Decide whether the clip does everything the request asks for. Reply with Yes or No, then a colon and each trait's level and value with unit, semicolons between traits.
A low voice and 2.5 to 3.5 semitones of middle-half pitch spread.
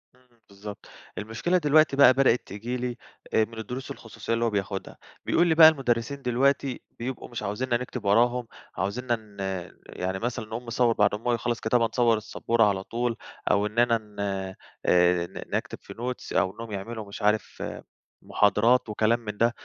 Yes: low, 115 Hz; average, 2.9 semitones